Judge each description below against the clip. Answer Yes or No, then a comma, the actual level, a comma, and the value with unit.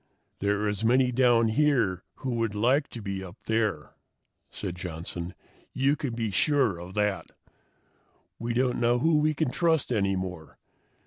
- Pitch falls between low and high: No, low, 115 Hz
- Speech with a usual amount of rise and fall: Yes, average, 5.0 semitones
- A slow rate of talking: No, average, 165 wpm